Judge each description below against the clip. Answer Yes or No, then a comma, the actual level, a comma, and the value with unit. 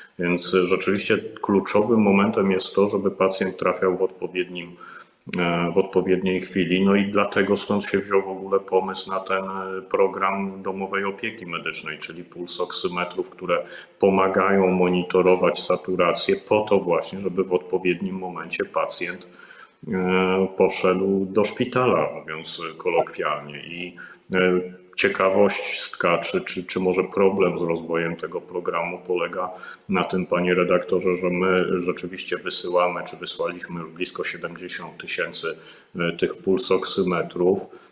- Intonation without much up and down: Yes, narrow, 1.2 semitones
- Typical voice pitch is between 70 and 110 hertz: Yes, very low, 95 Hz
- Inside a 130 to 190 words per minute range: No, average, 120 wpm